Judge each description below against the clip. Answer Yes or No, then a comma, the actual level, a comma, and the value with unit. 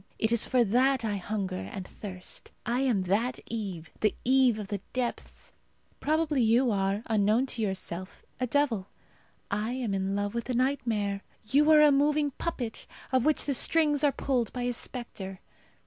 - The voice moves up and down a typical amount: Yes, average, 4.7 semitones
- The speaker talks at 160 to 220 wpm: Yes, average, 175 wpm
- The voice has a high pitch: Yes, high, 235 Hz